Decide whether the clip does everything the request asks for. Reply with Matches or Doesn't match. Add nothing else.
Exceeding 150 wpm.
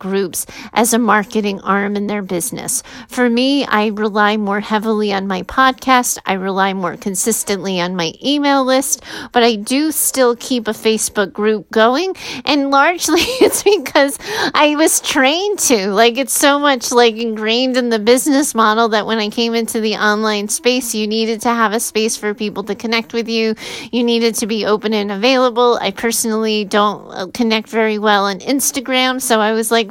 Matches